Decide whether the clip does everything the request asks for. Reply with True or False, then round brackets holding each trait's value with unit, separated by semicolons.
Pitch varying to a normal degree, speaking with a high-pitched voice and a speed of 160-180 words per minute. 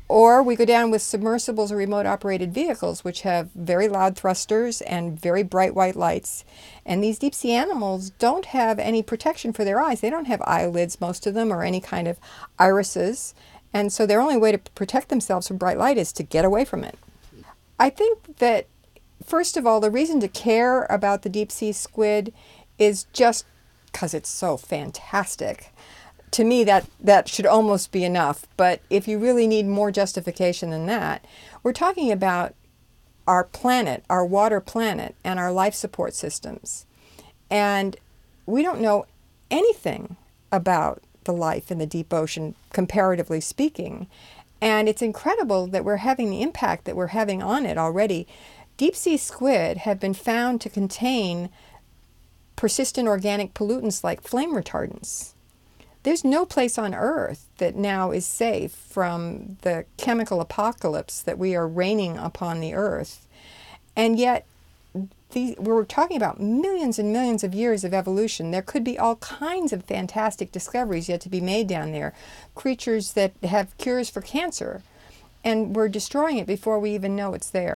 True (3.9 semitones; 210 Hz; 165 wpm)